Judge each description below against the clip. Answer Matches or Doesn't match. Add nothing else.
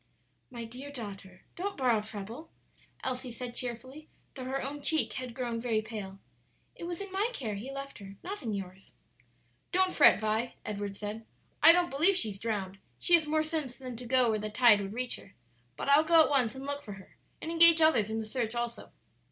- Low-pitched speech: Doesn't match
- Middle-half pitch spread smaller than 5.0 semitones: Doesn't match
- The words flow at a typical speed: Doesn't match